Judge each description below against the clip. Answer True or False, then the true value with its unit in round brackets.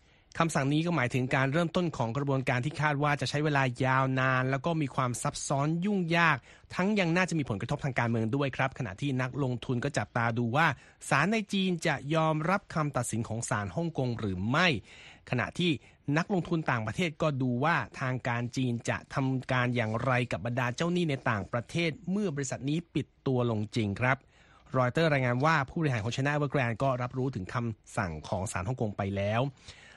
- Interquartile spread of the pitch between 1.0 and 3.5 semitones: False (4.6 semitones)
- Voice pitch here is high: False (135 Hz)